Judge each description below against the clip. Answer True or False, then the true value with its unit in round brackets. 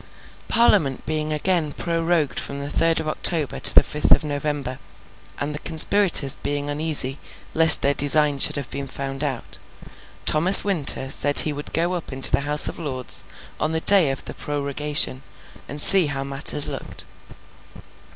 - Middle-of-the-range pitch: True (150 Hz)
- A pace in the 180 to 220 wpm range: False (165 wpm)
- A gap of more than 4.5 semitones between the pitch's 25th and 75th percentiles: False (2.5 semitones)